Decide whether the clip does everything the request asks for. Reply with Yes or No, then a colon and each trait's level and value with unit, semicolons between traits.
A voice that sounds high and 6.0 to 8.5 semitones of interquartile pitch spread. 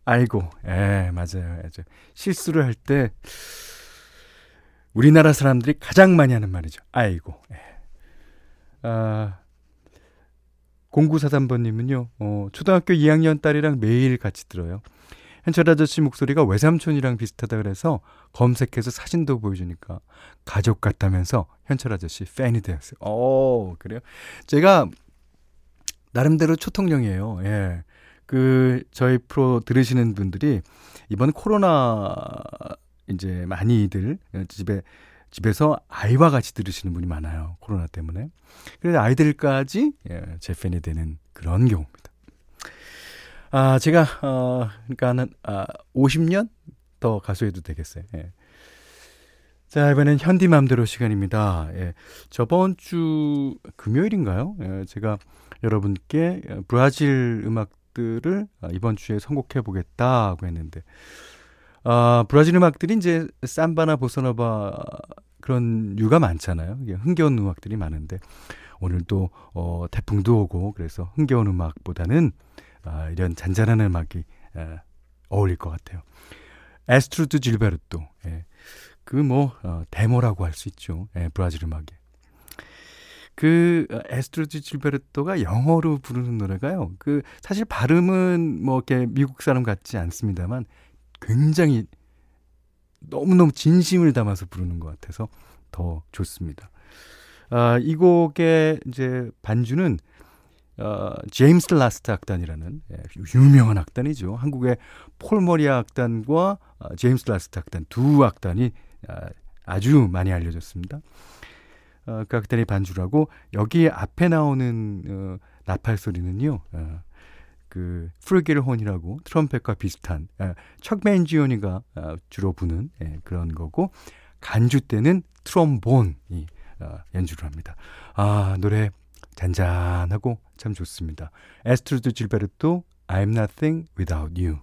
No: low, 110 Hz; wide, 7.7 semitones